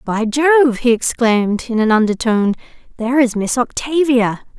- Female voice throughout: Yes, female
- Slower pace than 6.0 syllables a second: Yes, 5.0 syllables/s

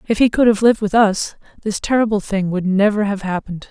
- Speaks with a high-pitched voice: Yes, high, 205 Hz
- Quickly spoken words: Yes, fast, 225 wpm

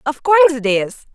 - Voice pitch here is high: Yes, very high, 275 Hz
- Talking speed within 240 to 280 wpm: No, fast, 210 wpm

